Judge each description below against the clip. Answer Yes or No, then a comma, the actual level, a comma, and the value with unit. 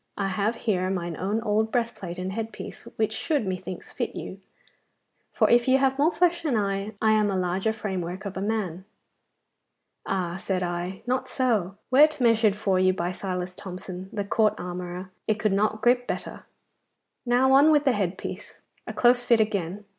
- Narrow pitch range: No, average, 4.0 semitones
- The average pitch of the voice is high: Yes, high, 205 Hz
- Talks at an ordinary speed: Yes, average, 185 wpm